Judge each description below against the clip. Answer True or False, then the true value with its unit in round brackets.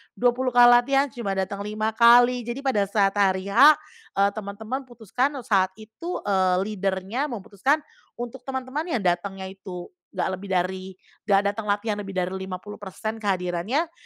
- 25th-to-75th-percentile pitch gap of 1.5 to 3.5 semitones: False (4.2 semitones)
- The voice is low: False (210 Hz)